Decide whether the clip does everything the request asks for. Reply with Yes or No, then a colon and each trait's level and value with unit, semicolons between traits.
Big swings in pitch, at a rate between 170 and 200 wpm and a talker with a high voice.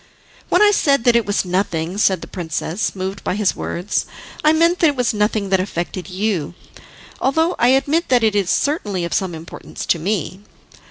Yes: wide, 6.0 semitones; average, 195 wpm; high, 205 Hz